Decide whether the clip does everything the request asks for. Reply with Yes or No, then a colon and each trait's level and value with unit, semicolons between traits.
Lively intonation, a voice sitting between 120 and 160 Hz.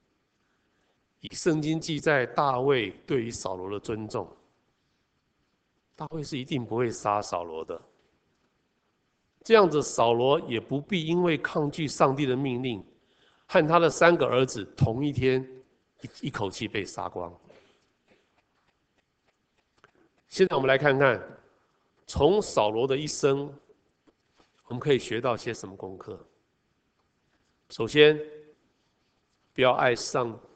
No: average, 4.0 semitones; medium, 140 Hz